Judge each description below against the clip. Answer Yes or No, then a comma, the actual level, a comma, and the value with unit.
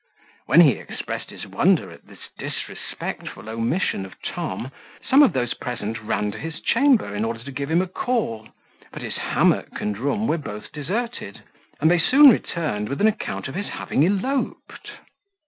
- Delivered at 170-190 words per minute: Yes, average, 175 wpm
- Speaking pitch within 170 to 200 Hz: No, medium, 150 Hz